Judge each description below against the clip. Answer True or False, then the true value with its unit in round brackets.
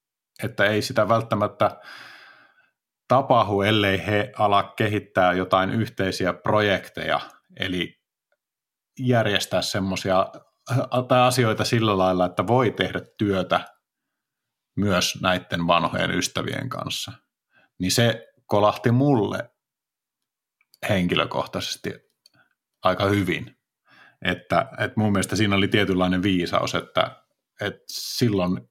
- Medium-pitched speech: False (100 Hz)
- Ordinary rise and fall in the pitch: True (3.4 semitones)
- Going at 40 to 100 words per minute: True (95 wpm)